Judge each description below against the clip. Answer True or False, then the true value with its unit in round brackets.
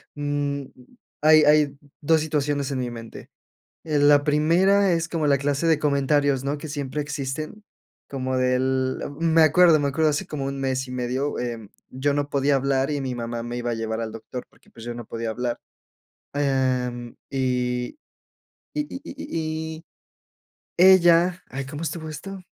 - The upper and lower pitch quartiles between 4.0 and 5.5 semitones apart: False (3.4 semitones)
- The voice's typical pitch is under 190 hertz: True (140 Hz)